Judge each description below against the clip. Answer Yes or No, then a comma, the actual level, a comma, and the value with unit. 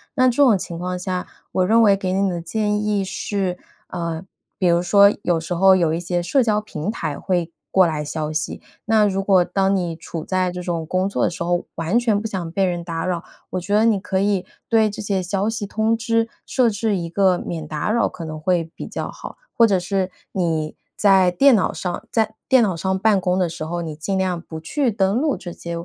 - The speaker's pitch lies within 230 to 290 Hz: No, medium, 185 Hz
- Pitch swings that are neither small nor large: Yes, average, 3.3 semitones